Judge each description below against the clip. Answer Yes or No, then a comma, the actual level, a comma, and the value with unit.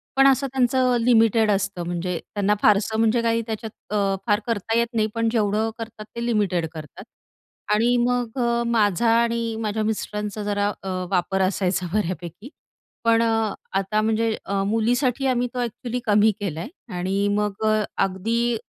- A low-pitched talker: No, high, 215 Hz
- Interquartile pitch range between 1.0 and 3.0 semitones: Yes, narrow, 2.6 semitones